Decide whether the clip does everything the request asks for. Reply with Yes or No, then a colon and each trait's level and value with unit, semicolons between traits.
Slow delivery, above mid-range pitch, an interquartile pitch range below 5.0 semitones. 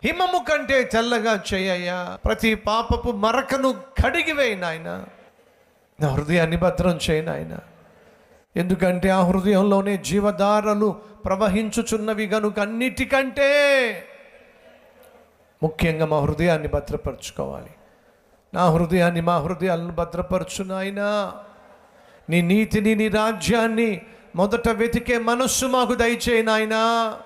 No: average, 85 wpm; high, 210 Hz; average, 4.3 semitones